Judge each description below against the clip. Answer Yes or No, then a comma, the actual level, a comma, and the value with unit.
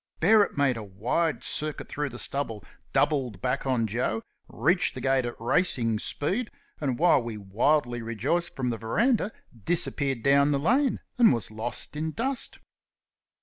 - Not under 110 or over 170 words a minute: Yes, average, 155 wpm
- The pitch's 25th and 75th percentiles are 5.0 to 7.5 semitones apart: Yes, wide, 5.6 semitones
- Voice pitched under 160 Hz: Yes, low, 135 Hz